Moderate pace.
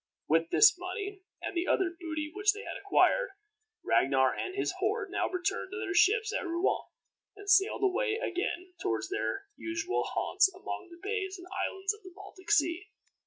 Yes: average, 175 wpm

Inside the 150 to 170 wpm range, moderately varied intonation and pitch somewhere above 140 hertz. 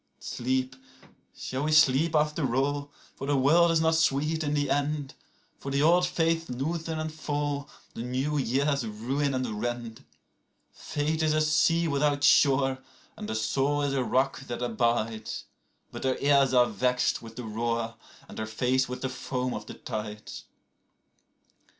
No: average, 155 wpm; average, 3.4 semitones; low, 135 Hz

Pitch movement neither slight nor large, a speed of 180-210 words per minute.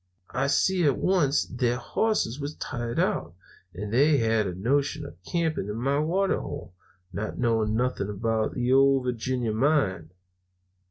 No: average, 4.7 semitones; average, 155 wpm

